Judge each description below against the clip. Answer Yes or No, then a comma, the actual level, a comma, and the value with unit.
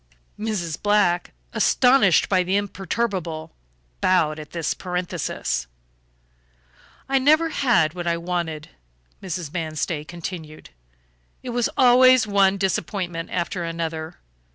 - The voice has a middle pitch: Yes, medium, 180 Hz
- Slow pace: Yes, slow, 105 wpm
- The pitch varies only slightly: No, average, 4.0 semitones